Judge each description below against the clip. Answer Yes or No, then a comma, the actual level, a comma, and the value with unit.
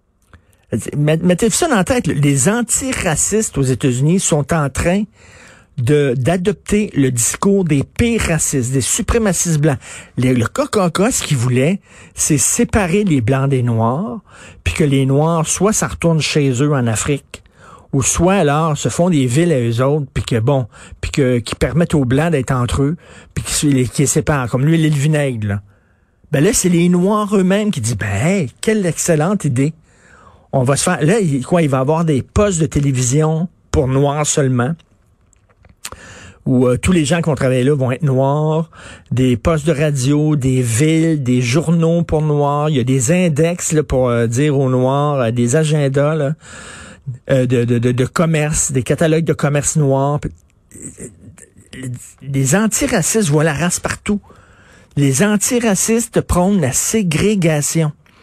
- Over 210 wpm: No, average, 170 wpm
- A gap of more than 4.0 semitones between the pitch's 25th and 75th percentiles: Yes, average, 4.7 semitones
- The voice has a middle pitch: Yes, medium, 145 Hz